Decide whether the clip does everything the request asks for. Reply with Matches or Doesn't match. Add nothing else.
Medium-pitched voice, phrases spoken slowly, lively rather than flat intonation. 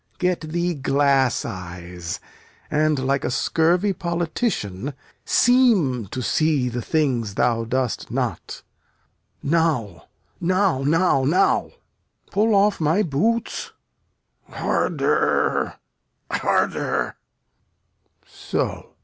Matches